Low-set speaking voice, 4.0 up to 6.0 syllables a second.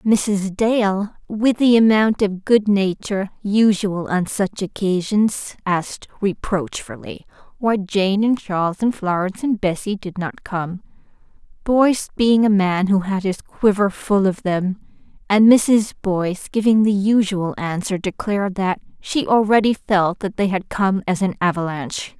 No: high, 200 Hz; 4.2 syllables/s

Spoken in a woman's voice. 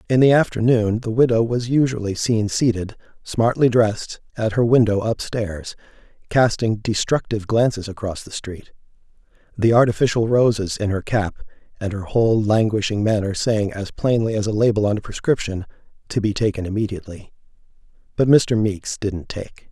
No: male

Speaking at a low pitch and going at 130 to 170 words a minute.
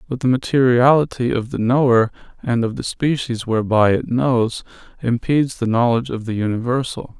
Yes: low, 120 Hz; average, 160 wpm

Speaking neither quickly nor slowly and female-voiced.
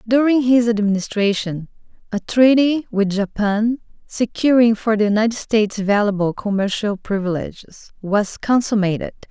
No: slow, 110 wpm; female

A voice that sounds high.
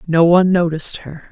No: medium, 165 Hz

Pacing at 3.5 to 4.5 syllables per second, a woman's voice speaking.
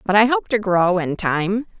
Yes: 4.4 syllables/s; female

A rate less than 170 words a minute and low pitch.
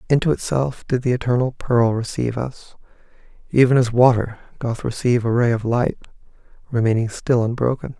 Yes: average, 150 wpm; low, 120 Hz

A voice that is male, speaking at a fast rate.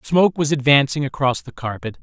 No: male; average, 180 wpm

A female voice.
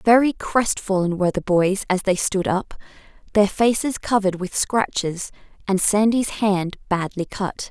Yes: female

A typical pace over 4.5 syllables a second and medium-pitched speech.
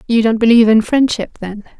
No: 6.2 syllables/s; high, 225 Hz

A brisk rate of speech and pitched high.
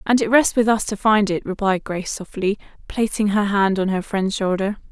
Yes: fast, 220 wpm; high, 205 Hz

